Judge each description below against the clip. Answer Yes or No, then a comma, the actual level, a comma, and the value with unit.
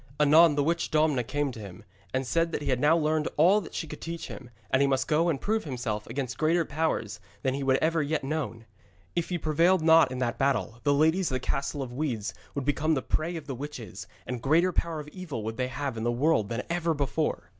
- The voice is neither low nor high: Yes, medium, 145 Hz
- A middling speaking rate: No, fast, 240 wpm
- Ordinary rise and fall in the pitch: Yes, average, 4.0 semitones